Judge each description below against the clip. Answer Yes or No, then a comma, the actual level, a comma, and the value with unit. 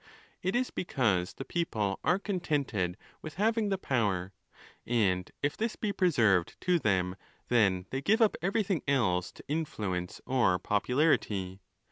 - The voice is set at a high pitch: No, low, 125 Hz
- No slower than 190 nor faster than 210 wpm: No, average, 140 wpm